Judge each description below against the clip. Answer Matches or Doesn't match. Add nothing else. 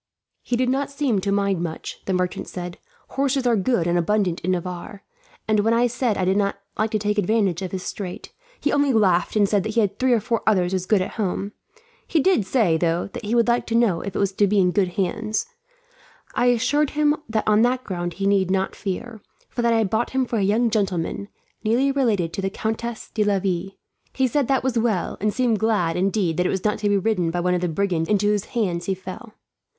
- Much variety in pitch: Doesn't match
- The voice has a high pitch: Matches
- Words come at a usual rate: Doesn't match